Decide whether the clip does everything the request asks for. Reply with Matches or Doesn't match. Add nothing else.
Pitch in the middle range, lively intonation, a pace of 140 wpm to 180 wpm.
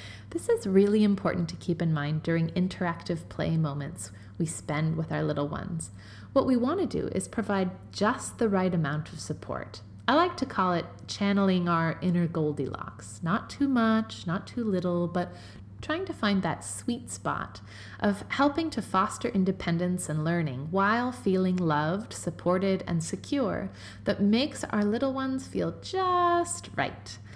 Matches